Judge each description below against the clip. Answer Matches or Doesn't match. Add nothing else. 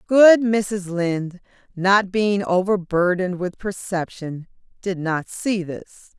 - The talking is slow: Matches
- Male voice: Doesn't match